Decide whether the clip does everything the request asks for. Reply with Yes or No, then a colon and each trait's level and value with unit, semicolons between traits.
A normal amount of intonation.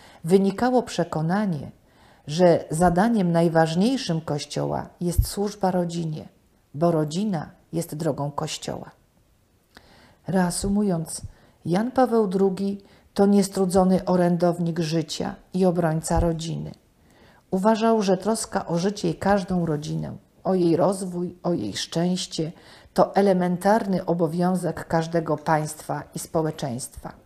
Yes: average, 3.1 semitones